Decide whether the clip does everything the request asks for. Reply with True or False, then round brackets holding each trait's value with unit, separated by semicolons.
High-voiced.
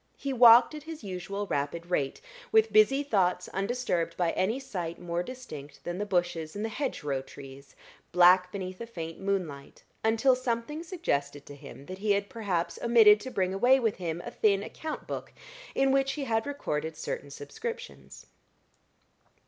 True (195 Hz)